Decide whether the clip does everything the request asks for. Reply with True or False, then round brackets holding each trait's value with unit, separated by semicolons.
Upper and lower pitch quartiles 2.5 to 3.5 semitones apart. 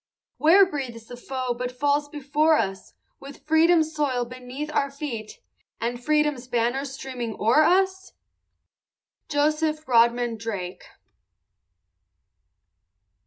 False (4.0 semitones)